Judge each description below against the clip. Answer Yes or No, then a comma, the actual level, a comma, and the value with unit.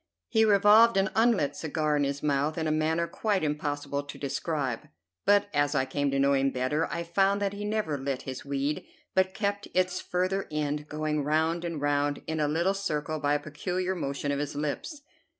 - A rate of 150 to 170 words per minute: No, average, 200 wpm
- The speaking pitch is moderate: Yes, medium, 155 Hz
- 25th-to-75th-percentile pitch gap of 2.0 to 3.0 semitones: No, average, 4.6 semitones